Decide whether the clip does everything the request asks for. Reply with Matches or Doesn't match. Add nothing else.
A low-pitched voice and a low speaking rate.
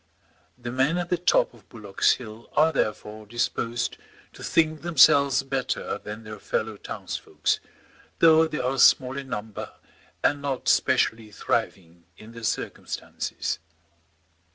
Matches